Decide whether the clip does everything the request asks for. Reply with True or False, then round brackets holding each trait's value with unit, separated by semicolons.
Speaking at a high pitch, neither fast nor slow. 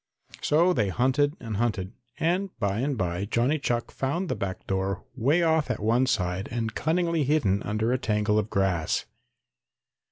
False (120 Hz; 165 wpm)